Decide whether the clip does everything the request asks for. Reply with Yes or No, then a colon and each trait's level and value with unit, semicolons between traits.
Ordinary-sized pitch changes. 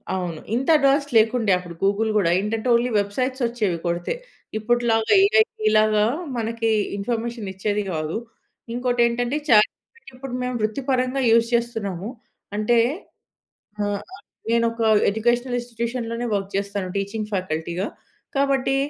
Yes: average, 3.3 semitones